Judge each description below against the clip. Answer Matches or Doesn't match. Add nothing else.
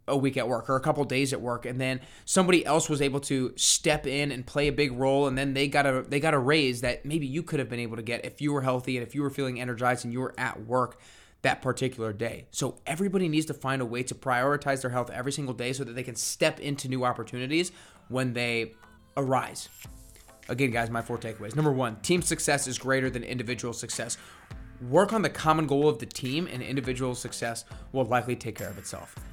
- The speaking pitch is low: Matches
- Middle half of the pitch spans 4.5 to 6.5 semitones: Doesn't match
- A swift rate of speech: Matches